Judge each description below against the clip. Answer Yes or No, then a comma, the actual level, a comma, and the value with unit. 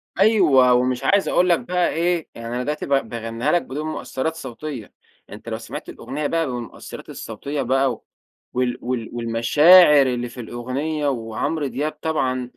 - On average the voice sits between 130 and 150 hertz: Yes, low, 135 Hz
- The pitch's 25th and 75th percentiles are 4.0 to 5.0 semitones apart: Yes, average, 4.3 semitones